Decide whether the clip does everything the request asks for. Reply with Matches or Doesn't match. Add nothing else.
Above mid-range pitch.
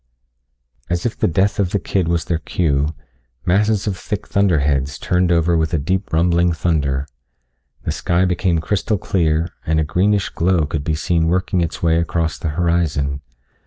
Doesn't match